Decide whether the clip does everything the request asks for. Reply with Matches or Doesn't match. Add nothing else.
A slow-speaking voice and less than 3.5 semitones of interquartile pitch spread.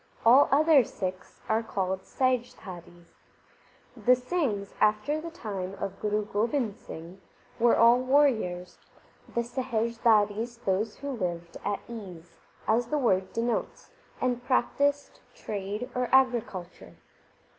Doesn't match